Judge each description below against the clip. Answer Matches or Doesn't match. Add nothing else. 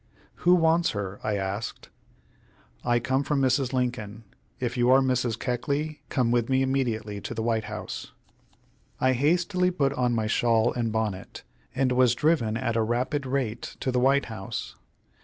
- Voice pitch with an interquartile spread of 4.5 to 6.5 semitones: Doesn't match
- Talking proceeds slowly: Doesn't match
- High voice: Doesn't match